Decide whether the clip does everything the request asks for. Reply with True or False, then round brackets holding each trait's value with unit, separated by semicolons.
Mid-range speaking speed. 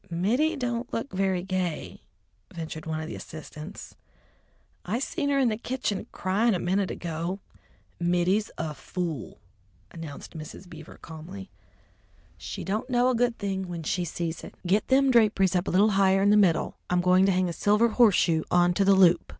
True (180 wpm)